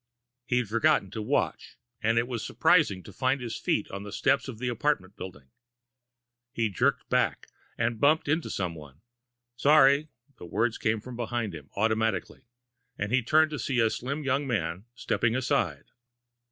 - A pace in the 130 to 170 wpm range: Yes, average, 160 wpm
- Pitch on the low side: Yes, low, 115 Hz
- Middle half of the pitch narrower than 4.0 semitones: No, average, 4.6 semitones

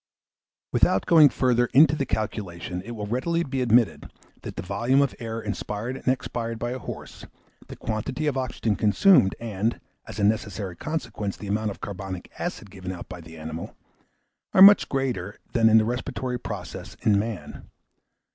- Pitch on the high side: No, low, 110 Hz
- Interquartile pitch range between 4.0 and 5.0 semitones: Yes, average, 4.3 semitones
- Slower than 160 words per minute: No, average, 170 wpm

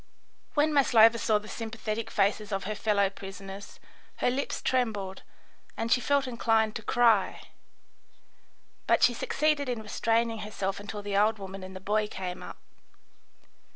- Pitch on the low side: No, high, 215 Hz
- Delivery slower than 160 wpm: Yes, average, 150 wpm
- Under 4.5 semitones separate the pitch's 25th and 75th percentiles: Yes, narrow, 2.6 semitones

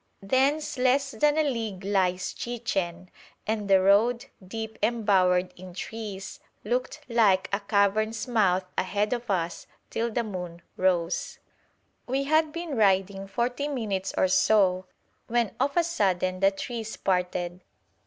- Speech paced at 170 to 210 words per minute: No, slow, 135 wpm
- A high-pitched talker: Yes, high, 210 Hz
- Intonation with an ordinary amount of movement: Yes, average, 4.4 semitones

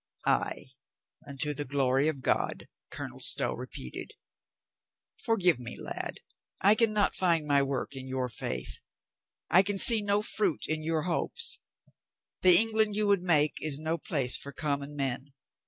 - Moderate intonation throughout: No, wide, 6.1 semitones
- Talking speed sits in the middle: Yes, average, 160 wpm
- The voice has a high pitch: No, medium, 155 Hz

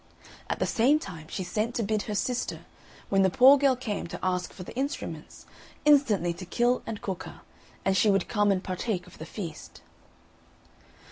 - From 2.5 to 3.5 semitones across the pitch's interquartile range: No, average, 4.9 semitones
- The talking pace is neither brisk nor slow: Yes, average, 190 wpm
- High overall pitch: Yes, high, 205 Hz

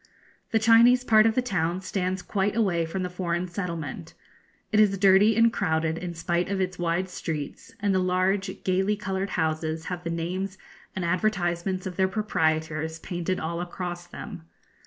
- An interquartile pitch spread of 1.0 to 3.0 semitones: Yes, average, 2.7 semitones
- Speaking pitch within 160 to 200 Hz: Yes, medium, 185 Hz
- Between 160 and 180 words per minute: Yes, average, 170 wpm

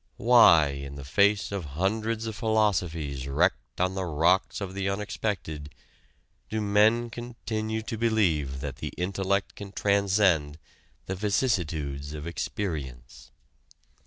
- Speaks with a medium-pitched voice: No, very low, 95 Hz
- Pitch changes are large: Yes, wide, 6.0 semitones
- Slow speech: Yes, slow, 125 wpm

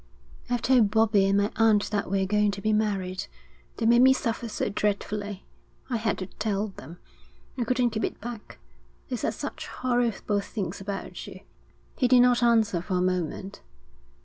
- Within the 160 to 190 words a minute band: Yes, average, 175 wpm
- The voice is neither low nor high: No, high, 210 Hz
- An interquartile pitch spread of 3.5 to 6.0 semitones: No, average, 2.9 semitones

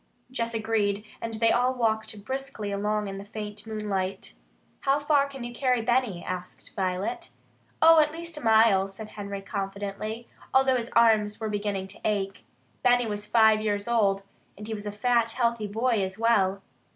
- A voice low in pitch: No, high, 220 Hz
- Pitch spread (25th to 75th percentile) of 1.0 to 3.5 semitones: Yes, average, 2.9 semitones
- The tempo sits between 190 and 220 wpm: No, average, 175 wpm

